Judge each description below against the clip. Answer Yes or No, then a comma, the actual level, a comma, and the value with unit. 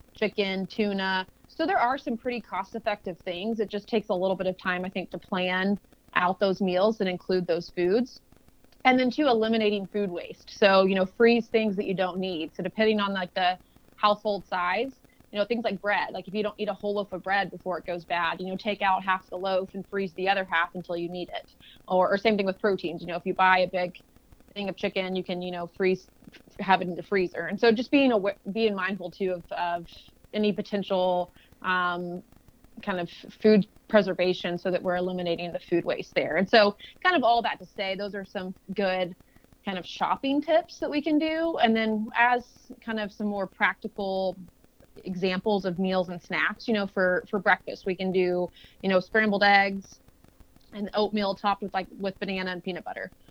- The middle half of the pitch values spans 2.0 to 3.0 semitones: Yes, narrow, 2.5 semitones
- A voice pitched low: No, high, 195 Hz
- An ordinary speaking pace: No, fast, 215 wpm